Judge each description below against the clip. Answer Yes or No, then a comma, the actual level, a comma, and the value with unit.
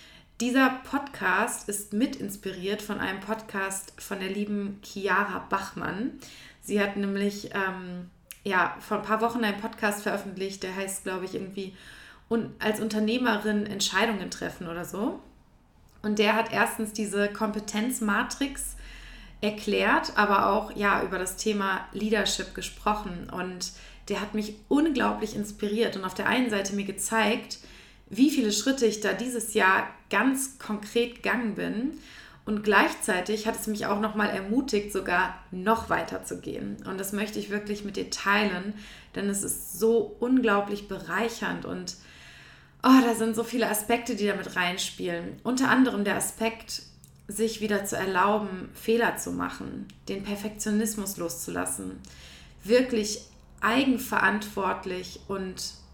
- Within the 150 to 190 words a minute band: No, average, 140 wpm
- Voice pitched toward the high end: Yes, high, 210 Hz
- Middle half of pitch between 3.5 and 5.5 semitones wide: No, narrow, 2.6 semitones